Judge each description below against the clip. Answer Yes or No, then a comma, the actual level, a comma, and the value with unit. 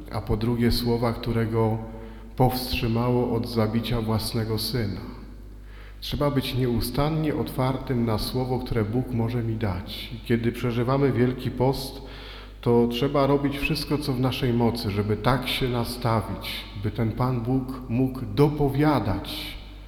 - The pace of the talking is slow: No, average, 135 wpm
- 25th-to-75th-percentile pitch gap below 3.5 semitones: Yes, narrow, 2.5 semitones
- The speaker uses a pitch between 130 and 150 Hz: No, low, 120 Hz